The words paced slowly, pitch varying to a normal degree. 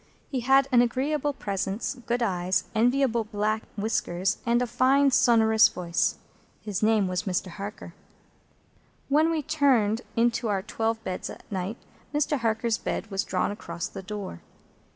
No: average, 150 wpm; average, 4.0 semitones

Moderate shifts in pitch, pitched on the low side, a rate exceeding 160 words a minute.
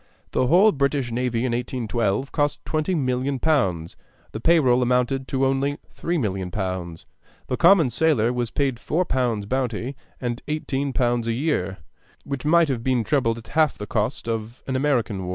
Yes: average, 3.8 semitones; low, 125 Hz; average, 170 wpm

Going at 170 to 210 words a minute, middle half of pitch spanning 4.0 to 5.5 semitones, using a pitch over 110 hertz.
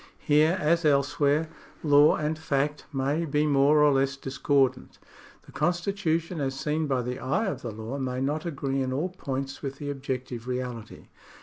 No: average, 175 wpm; narrow, 2.6 semitones; medium, 140 Hz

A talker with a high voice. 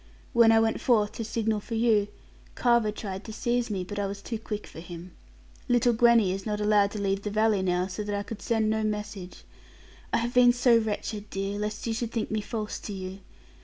Yes: high, 215 Hz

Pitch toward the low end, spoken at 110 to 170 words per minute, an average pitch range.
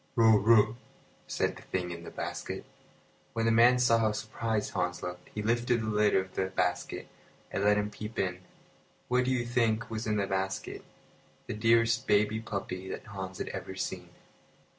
No: low, 105 Hz; average, 185 wpm; average, 3.1 semitones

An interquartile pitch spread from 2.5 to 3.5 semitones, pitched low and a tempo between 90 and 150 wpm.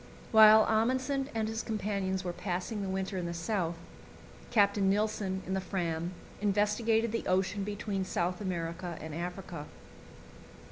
No: average, 3.1 semitones; high, 195 Hz; average, 140 wpm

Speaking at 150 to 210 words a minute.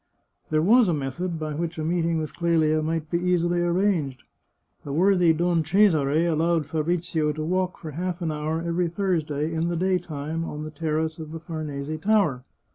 Yes: average, 180 wpm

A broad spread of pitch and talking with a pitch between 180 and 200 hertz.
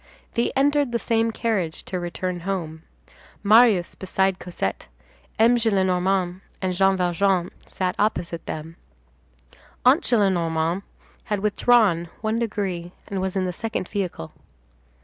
No: average, 3.7 semitones; high, 190 Hz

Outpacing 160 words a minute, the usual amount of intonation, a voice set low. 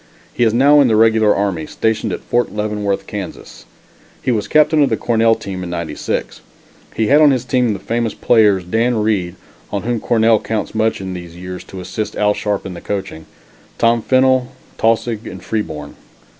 Yes: average, 185 wpm; average, 3.4 semitones; low, 110 Hz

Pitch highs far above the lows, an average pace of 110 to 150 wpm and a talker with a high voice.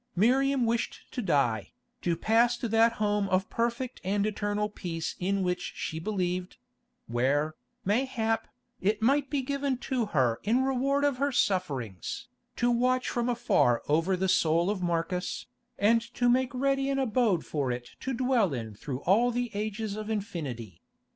No: wide, 6.1 semitones; average, 160 wpm; high, 210 Hz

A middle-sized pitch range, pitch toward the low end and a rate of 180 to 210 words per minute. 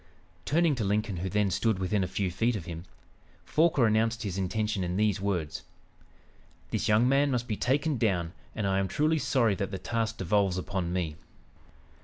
Yes: average, 3.7 semitones; low, 105 Hz; average, 185 wpm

